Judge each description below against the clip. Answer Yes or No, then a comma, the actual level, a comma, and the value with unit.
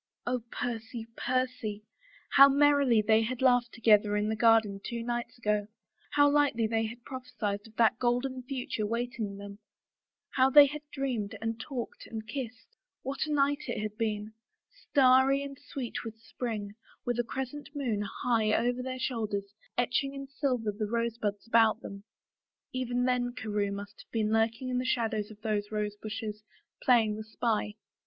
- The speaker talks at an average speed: Yes, average, 165 wpm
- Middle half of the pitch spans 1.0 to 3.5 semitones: Yes, average, 3.1 semitones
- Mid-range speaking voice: No, high, 230 Hz